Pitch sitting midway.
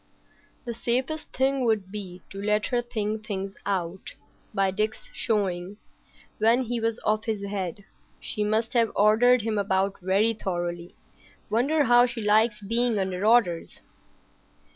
No: high, 215 Hz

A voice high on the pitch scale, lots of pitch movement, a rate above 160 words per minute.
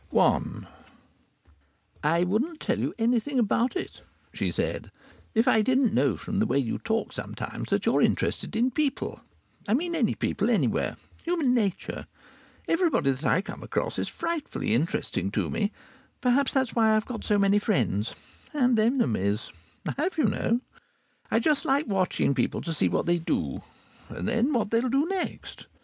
Yes: high, 225 Hz; wide, 6.0 semitones; average, 170 wpm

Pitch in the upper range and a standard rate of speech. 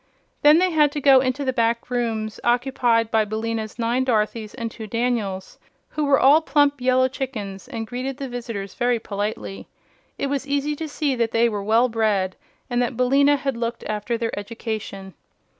Yes: high, 240 Hz; average, 180 wpm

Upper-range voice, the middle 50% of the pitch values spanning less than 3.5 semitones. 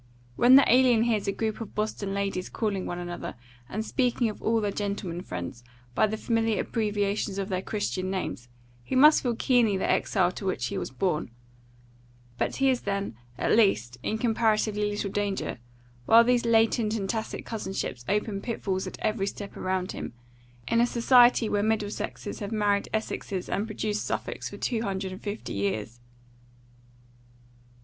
Yes: high, 205 Hz; average, 2.8 semitones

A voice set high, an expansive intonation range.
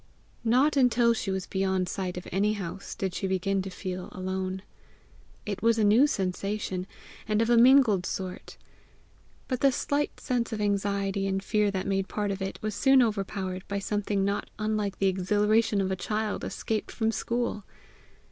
No: high, 200 Hz; narrow, 2.6 semitones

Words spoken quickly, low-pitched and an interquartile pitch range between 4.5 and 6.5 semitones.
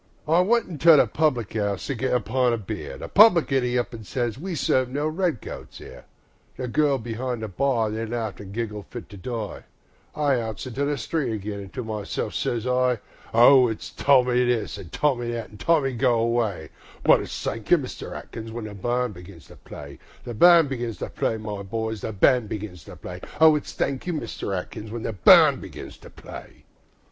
No: fast, 210 wpm; low, 120 Hz; average, 3.9 semitones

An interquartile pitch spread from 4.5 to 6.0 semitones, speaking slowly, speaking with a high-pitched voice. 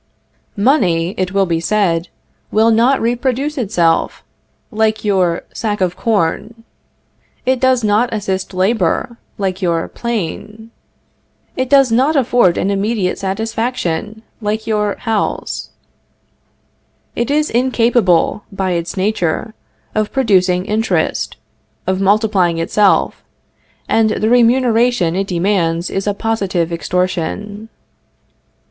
No: average, 3.8 semitones; slow, 110 wpm; high, 210 Hz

